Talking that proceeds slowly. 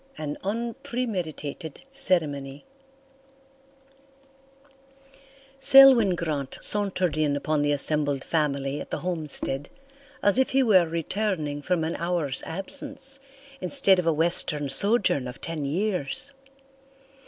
Yes: slow, 110 wpm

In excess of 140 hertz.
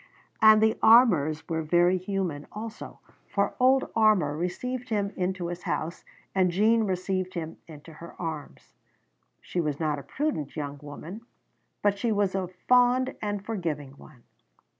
Yes: medium, 185 Hz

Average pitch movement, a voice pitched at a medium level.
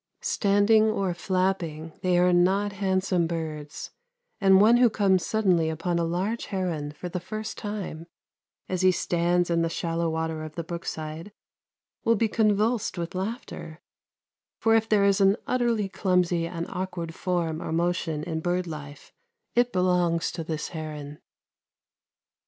Yes: average, 3.4 semitones; medium, 180 Hz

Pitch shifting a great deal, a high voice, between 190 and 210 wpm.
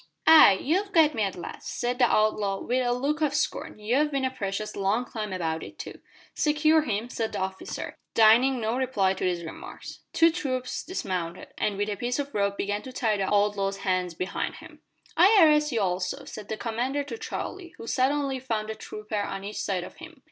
Yes: wide, 5.8 semitones; high, 225 Hz; fast, 205 wpm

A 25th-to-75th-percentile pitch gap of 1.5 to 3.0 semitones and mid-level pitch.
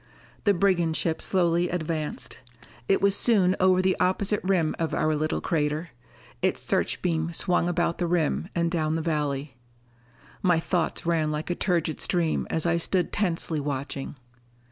Yes: narrow, 2.5 semitones; medium, 170 Hz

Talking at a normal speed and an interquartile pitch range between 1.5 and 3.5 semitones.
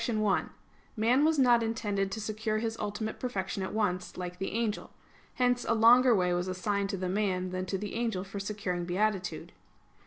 Yes: average, 180 wpm; average, 3.2 semitones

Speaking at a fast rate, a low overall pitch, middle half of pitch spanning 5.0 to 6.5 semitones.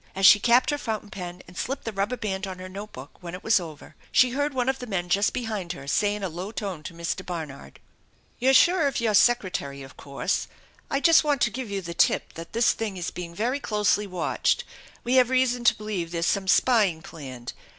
No: fast, 235 wpm; high, 200 Hz; wide, 5.6 semitones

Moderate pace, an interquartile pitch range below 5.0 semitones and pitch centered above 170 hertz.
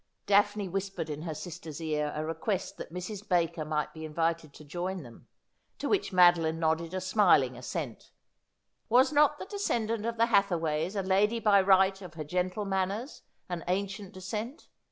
Yes: average, 170 wpm; average, 4.1 semitones; medium, 185 Hz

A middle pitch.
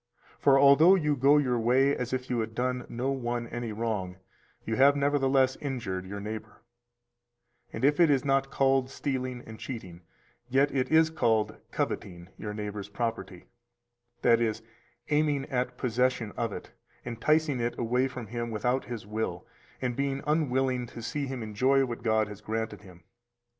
No: low, 125 Hz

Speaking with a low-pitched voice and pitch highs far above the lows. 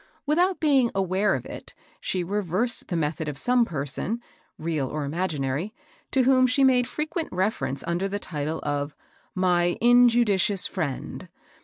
No: high, 190 Hz; wide, 7.6 semitones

